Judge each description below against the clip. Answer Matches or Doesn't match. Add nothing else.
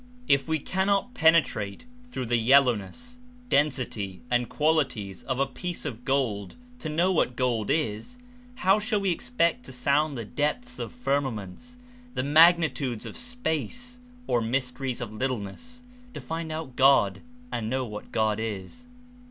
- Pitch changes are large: Matches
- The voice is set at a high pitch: Doesn't match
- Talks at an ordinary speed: Matches